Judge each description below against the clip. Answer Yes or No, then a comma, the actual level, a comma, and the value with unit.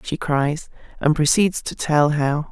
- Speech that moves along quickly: No, average, 165 wpm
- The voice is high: No, medium, 150 Hz